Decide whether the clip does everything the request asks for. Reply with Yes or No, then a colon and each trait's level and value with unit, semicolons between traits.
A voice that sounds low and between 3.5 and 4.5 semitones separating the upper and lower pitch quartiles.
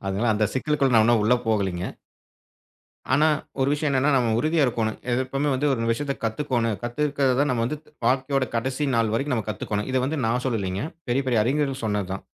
Yes: low, 125 Hz; average, 4.0 semitones